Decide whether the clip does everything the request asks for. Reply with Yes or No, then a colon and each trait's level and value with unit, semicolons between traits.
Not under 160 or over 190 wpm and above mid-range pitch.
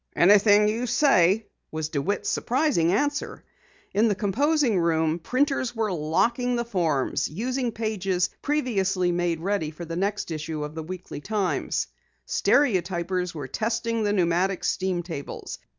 No: slow, 135 wpm; high, 195 Hz